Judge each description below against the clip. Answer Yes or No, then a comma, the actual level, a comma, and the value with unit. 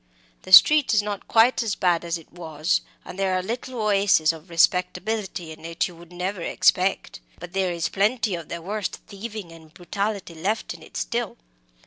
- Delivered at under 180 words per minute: No, average, 185 wpm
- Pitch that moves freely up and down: No, average, 3.5 semitones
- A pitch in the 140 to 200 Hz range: Yes, medium, 185 Hz